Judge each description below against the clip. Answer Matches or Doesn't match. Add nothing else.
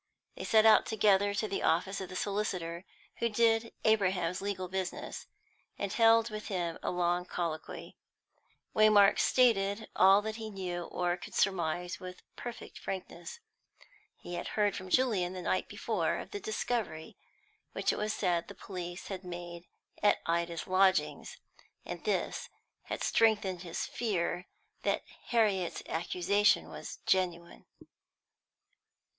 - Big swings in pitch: Doesn't match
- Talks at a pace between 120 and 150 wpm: Matches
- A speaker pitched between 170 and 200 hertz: Matches